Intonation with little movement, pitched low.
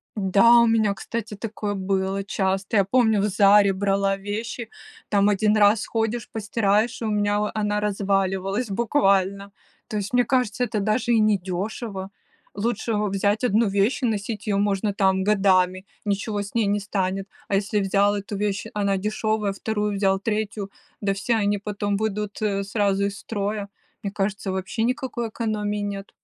No: narrow, 1.6 semitones; high, 205 Hz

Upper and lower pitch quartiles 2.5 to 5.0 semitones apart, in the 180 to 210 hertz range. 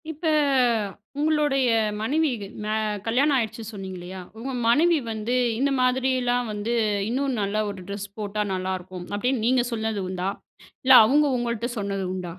No: average, 4.6 semitones; high, 230 Hz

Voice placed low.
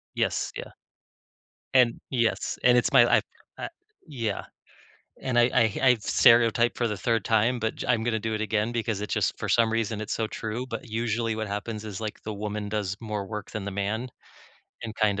Yes: low, 110 Hz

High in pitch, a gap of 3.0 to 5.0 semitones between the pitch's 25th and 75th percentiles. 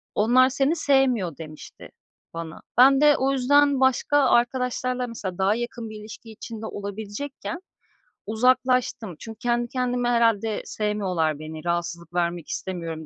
No: high, 230 Hz; wide, 5.4 semitones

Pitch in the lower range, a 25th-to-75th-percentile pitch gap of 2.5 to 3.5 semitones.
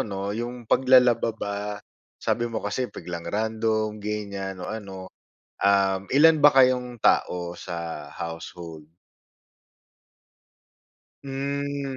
No: low, 110 Hz; average, 4.6 semitones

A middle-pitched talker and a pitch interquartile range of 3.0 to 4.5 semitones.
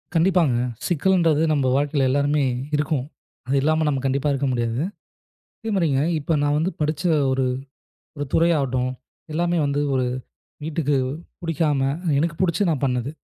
Yes: medium, 145 Hz; average, 3.3 semitones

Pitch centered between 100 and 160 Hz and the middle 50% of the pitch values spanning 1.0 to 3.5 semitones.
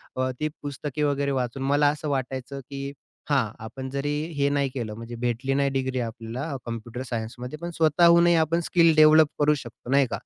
Yes: low, 135 Hz; average, 3.0 semitones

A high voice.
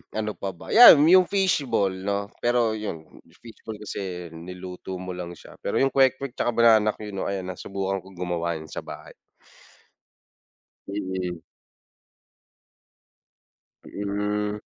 No: low, 100 Hz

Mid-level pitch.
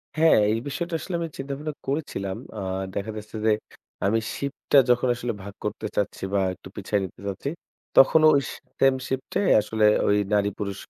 No: low, 120 Hz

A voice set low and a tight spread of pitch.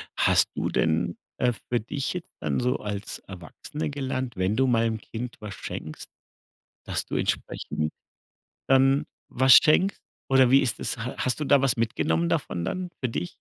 No: low, 125 Hz; average, 4.6 semitones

